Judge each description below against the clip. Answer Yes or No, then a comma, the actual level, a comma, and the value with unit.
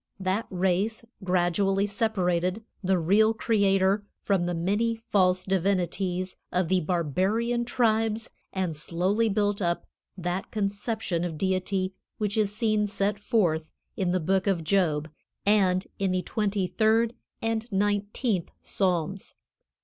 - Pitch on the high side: Yes, high, 195 Hz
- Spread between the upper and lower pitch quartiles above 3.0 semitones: No, average, 2.7 semitones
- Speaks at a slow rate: Yes, slow, 125 wpm